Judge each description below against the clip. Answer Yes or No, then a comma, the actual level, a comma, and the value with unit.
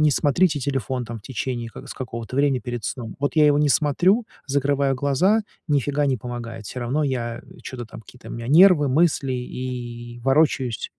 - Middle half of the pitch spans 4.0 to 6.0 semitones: No, average, 3.3 semitones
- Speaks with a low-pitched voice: Yes, low, 130 Hz